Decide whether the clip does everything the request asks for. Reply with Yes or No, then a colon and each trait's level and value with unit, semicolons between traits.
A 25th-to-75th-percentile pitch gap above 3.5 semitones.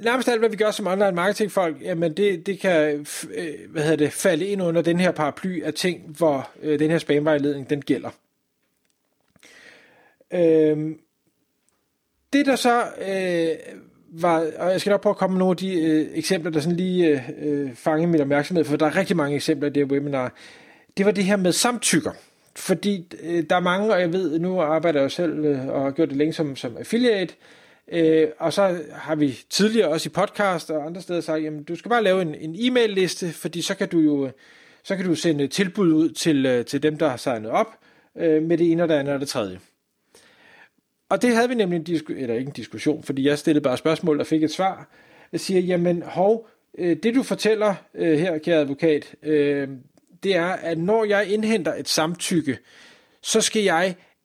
Yes: average, 3.9 semitones